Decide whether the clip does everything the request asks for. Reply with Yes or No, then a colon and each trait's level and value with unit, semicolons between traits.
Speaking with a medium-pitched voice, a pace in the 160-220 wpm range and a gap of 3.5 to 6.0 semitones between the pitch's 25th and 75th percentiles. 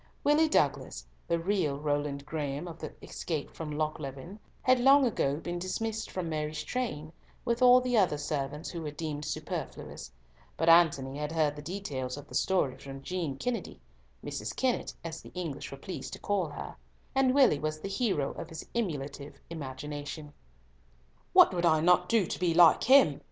Yes: medium, 160 Hz; average, 175 wpm; average, 4.7 semitones